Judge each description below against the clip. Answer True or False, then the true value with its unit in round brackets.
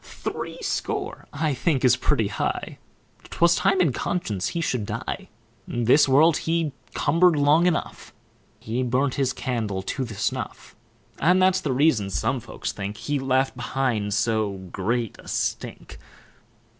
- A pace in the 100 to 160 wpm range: True (145 wpm)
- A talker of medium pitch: False (130 Hz)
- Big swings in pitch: True (5.7 semitones)